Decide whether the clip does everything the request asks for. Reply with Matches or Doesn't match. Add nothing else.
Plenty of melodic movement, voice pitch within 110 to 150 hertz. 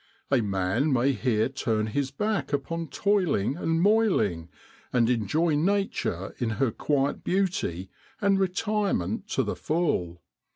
Matches